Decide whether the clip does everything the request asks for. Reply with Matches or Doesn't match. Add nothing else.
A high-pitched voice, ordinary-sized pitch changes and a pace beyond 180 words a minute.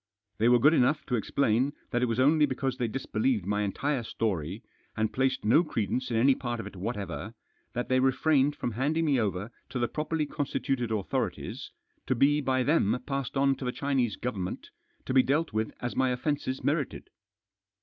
Doesn't match